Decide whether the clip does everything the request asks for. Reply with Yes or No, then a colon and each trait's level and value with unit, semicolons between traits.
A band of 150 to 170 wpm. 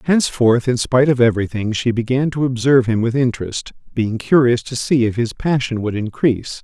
No: average, 190 wpm